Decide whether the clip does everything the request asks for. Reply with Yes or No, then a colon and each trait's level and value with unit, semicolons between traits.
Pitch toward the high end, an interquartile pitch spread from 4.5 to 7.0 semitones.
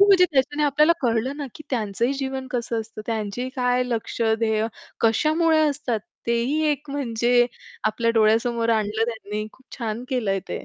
No: high, 240 Hz; average, 3.5 semitones